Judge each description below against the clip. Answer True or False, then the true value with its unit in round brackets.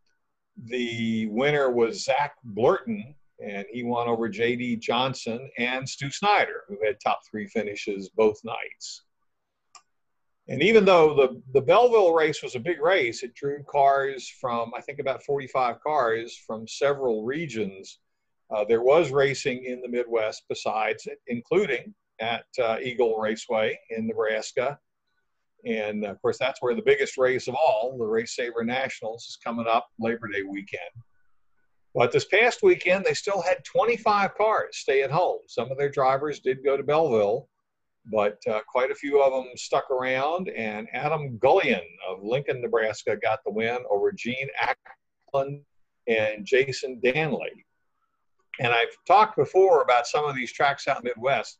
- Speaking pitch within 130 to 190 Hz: True (140 Hz)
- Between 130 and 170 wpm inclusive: True (160 wpm)